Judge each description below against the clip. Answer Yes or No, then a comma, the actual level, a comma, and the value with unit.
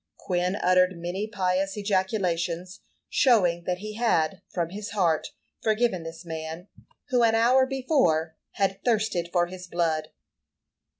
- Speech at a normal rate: No, slow, 130 wpm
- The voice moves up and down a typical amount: Yes, average, 3.8 semitones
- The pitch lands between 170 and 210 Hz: Yes, medium, 185 Hz